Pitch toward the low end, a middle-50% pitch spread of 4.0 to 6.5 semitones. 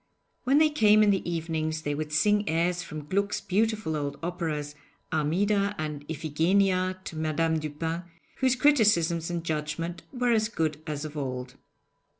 No: medium, 165 Hz; average, 4.7 semitones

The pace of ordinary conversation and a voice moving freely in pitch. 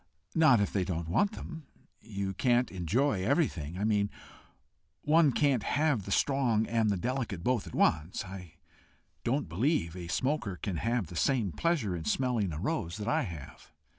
Yes: average, 170 wpm; wide, 6.7 semitones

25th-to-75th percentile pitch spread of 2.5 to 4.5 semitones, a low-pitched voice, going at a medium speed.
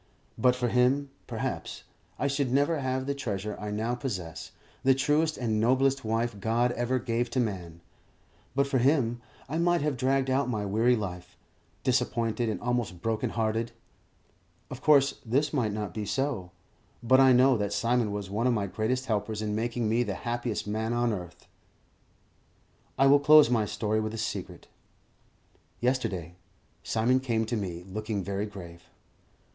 Yes: average, 3.7 semitones; low, 120 Hz; average, 165 wpm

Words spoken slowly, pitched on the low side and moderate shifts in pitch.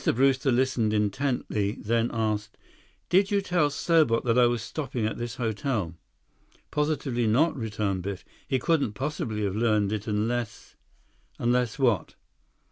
Yes: slow, 130 wpm; low, 120 Hz; average, 4.1 semitones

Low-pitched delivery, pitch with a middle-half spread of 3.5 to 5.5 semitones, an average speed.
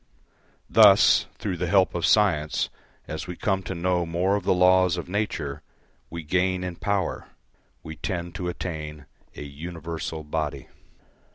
No: very low, 85 Hz; average, 2.8 semitones; average, 150 wpm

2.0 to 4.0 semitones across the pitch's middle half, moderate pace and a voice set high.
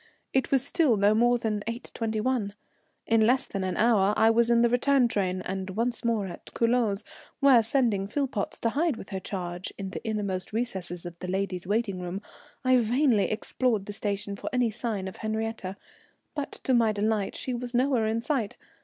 Yes: average, 3.5 semitones; average, 190 wpm; high, 220 Hz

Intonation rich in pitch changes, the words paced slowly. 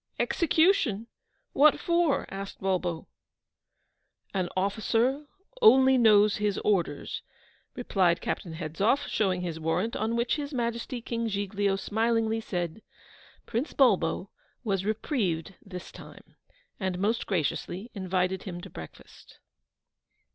No: average, 4.2 semitones; slow, 110 wpm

